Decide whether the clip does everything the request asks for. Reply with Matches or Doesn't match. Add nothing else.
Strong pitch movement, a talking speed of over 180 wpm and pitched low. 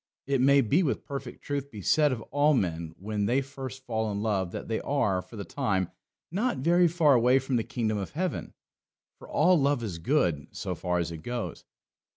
Matches